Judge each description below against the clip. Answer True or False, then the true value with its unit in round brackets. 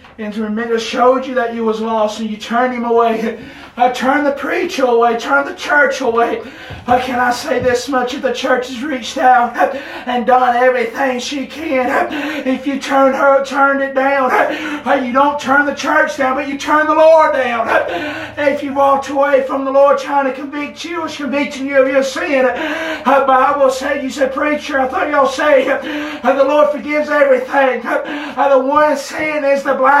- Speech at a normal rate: False (215 wpm)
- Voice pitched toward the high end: True (270 Hz)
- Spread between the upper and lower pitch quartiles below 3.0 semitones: True (2.4 semitones)